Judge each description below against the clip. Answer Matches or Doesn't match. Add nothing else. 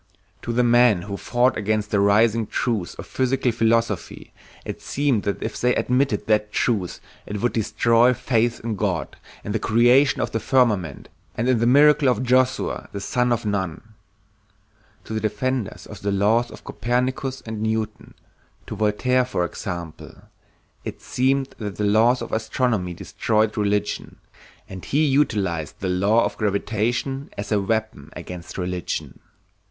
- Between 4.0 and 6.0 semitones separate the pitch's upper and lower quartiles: Doesn't match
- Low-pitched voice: Matches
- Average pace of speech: Matches